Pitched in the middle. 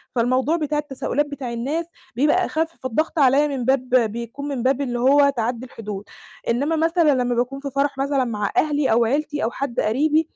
No: very high, 275 Hz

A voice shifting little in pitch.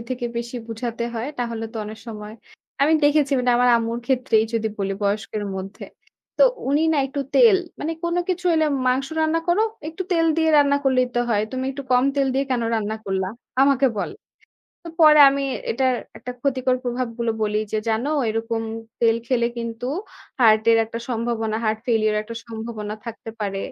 No: average, 3.6 semitones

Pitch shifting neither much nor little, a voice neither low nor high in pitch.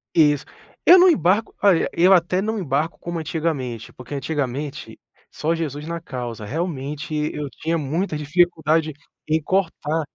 Yes: average, 3.1 semitones; medium, 160 Hz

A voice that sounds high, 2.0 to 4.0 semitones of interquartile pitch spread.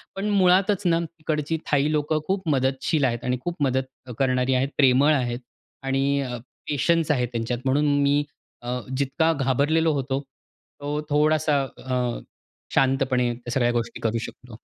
No: low, 135 Hz; average, 3.3 semitones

